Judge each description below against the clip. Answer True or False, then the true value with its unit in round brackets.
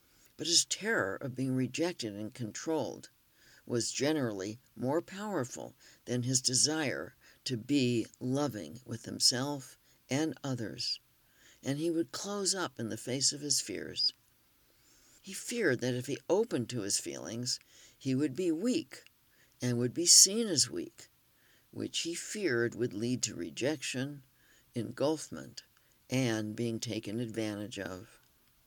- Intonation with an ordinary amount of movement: True (4.8 semitones)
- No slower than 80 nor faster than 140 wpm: True (135 wpm)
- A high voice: False (130 Hz)